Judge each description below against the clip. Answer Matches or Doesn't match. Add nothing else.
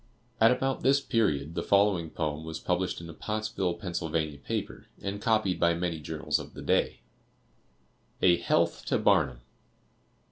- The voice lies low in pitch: Matches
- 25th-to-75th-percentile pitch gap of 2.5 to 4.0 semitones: Doesn't match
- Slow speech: Doesn't match